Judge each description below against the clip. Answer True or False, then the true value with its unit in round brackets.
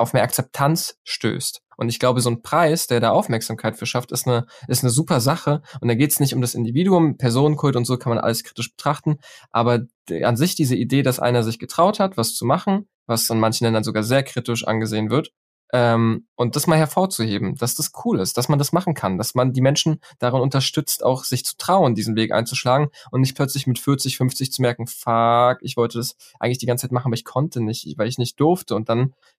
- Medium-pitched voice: False (125 Hz)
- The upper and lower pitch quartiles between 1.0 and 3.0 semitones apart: False (3.4 semitones)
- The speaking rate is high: True (235 wpm)